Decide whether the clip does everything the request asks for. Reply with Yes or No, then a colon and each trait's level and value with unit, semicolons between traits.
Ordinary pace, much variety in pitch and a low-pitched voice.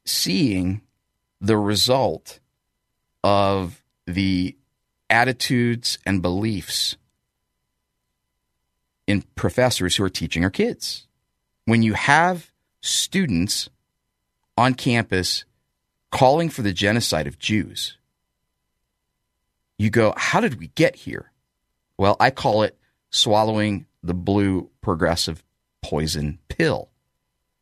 No: slow, 95 wpm; wide, 6.1 semitones; very low, 95 Hz